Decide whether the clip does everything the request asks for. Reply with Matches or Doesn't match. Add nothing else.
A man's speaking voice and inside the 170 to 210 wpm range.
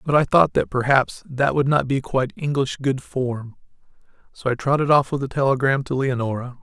Matches